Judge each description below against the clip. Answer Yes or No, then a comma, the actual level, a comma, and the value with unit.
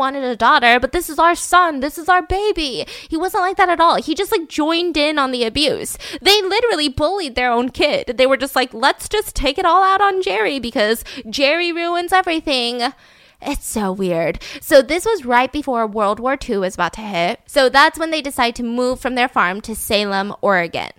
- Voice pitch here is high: Yes, very high, 280 Hz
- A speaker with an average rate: No, fast, 215 wpm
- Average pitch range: No, wide, 5.9 semitones